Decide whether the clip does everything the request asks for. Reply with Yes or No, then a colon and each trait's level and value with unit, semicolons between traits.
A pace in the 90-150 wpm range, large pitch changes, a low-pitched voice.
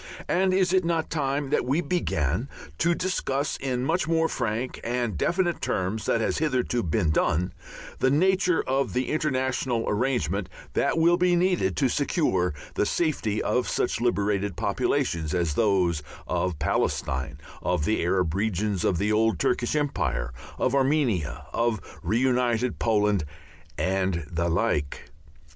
Yes: average, 145 wpm; wide, 7.9 semitones; low, 120 Hz